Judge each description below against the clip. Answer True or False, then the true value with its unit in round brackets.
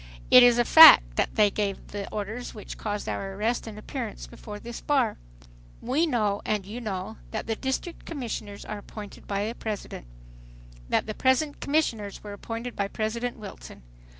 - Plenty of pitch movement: False (3.2 semitones)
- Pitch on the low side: False (215 Hz)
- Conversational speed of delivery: True (175 wpm)